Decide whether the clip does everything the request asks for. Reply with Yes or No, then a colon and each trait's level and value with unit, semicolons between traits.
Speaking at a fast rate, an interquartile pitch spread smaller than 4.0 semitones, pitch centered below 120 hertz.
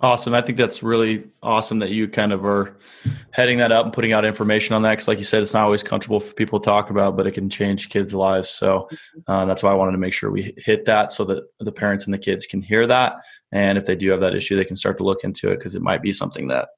Yes: fast, 290 wpm; average, 2.7 semitones; low, 105 Hz